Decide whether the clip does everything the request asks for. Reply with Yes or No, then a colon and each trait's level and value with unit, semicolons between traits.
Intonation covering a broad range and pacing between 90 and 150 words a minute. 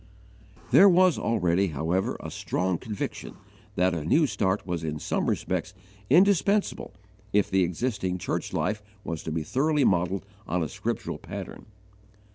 Yes: wide, 6.9 semitones; average, 145 wpm